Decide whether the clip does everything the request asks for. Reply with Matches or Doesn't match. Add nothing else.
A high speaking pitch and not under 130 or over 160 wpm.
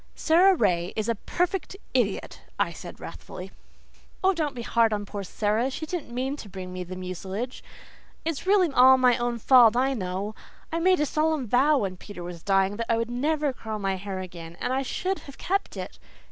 Doesn't match